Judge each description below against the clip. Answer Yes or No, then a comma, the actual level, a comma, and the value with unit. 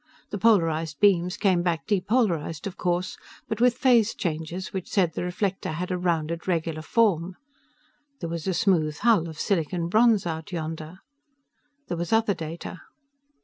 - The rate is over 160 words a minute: No, average, 155 wpm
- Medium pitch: Yes, medium, 175 Hz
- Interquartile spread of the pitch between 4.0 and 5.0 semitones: No, average, 3.5 semitones